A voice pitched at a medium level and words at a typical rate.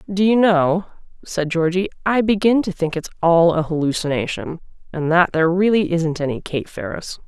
Yes: medium, 175 Hz; average, 175 wpm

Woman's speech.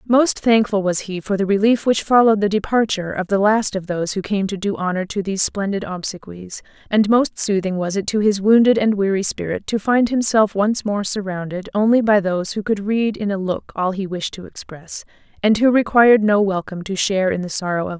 Yes: female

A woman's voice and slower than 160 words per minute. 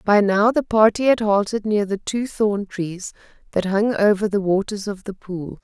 No: female; average, 200 wpm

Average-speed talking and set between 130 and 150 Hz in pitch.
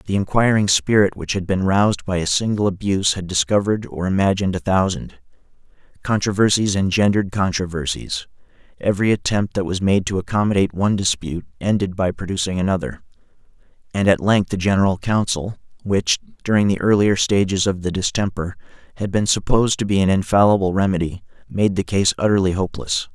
No: average, 155 wpm; very low, 95 Hz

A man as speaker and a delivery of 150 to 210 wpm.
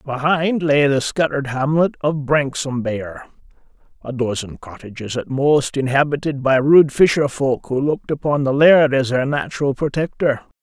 No: male; average, 140 wpm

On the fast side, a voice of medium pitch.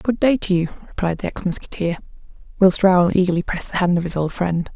Yes: fast, 225 wpm; medium, 180 Hz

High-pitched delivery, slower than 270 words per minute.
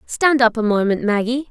Yes: high, 235 Hz; average, 200 wpm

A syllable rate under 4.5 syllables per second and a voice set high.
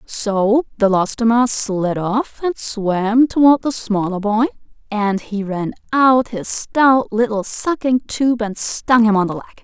Yes: 3.7 syllables/s; high, 225 Hz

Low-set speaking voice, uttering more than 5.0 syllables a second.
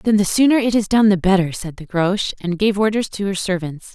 No: high, 195 Hz; 5.7 syllables/s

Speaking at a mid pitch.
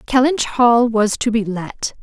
No: high, 230 Hz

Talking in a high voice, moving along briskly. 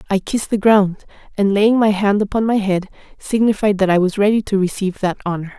Yes: high, 200 Hz; fast, 215 wpm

